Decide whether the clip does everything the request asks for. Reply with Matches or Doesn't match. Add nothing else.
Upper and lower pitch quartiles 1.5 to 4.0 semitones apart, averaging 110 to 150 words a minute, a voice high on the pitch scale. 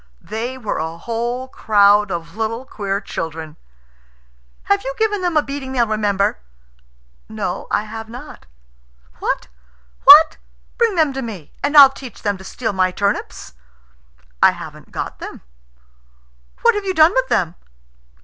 Doesn't match